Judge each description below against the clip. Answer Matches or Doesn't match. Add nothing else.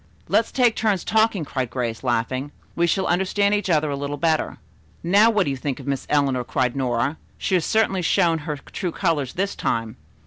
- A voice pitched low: Doesn't match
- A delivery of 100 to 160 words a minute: Doesn't match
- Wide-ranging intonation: Matches